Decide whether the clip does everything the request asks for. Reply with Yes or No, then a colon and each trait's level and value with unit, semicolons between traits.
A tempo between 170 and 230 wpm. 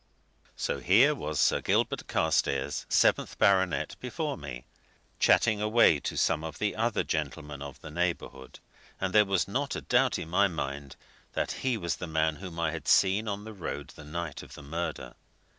Yes: average, 180 wpm